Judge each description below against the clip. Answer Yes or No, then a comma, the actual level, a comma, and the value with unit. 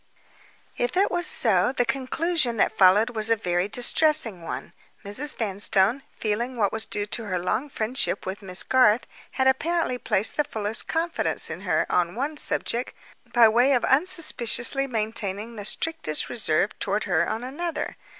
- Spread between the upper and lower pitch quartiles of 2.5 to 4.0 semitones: No, average, 4.7 semitones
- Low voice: No, high, 230 Hz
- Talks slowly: No, average, 160 wpm